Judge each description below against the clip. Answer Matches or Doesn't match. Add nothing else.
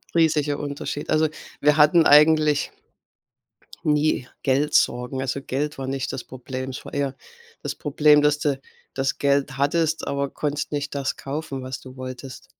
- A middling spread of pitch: Doesn't match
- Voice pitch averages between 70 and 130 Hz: Doesn't match